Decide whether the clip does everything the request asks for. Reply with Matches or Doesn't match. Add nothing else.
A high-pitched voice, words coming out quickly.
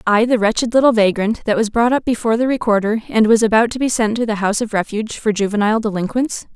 Matches